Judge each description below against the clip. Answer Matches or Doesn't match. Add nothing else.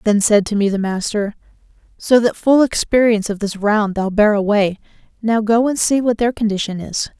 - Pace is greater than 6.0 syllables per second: Doesn't match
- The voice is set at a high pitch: Matches